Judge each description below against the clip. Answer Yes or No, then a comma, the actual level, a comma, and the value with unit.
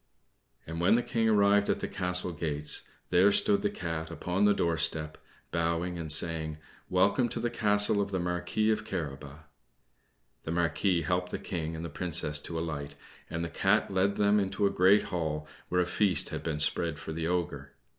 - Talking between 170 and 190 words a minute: Yes, average, 185 wpm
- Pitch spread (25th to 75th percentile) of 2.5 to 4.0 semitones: Yes, average, 3.7 semitones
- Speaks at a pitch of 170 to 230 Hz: No, very low, 90 Hz